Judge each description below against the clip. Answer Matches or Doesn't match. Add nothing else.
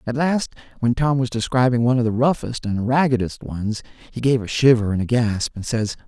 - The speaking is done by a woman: Doesn't match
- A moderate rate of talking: Doesn't match